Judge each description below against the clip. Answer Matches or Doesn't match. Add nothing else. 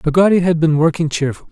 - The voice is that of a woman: Doesn't match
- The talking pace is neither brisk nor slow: Matches